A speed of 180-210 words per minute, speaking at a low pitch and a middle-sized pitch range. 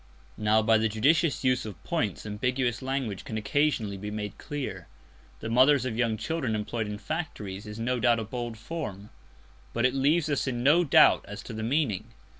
Yes: average, 190 wpm; low, 120 Hz; average, 4.1 semitones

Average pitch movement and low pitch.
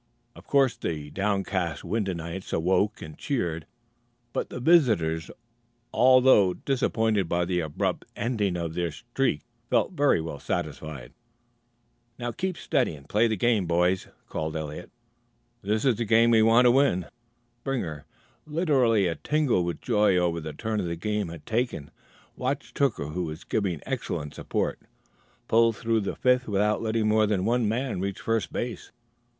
No: wide, 5.9 semitones; low, 105 Hz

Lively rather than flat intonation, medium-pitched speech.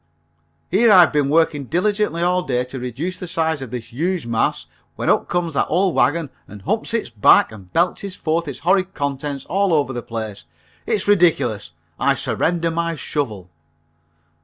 Yes: wide, 5.8 semitones; medium, 160 Hz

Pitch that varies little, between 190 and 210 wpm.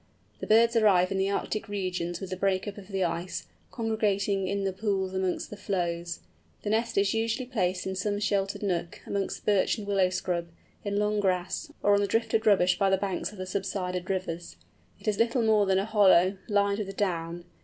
Yes: narrow, 2.1 semitones; fast, 205 wpm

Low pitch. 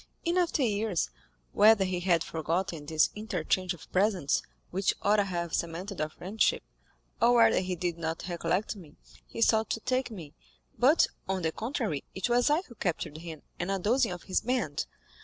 No: high, 190 Hz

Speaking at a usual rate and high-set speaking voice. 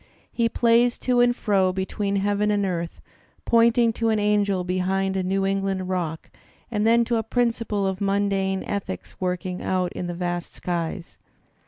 Yes: average, 170 wpm; high, 195 Hz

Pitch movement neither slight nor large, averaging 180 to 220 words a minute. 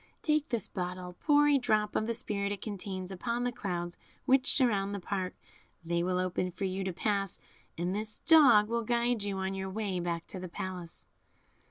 Yes: average, 4.2 semitones; average, 195 wpm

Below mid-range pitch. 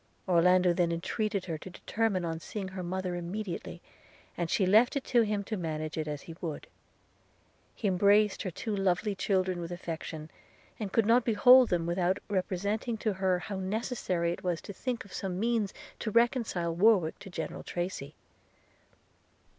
No: medium, 185 Hz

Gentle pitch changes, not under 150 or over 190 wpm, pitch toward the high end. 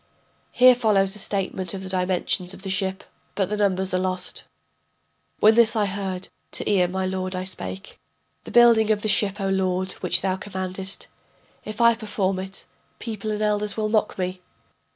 Yes: narrow, 2.2 semitones; average, 180 wpm; high, 195 Hz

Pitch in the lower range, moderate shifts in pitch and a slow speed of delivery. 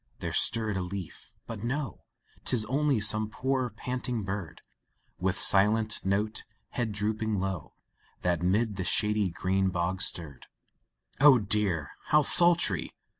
Yes: low, 105 Hz; average, 3.7 semitones; slow, 130 wpm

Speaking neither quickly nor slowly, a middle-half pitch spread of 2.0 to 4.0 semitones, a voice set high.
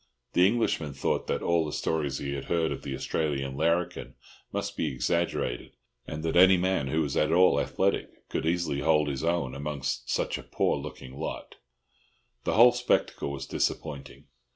No: average, 175 wpm; average, 3.7 semitones; very low, 75 Hz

